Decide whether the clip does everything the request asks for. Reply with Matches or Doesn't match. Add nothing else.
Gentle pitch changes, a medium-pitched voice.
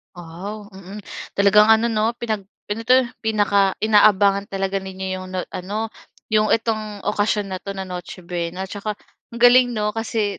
Doesn't match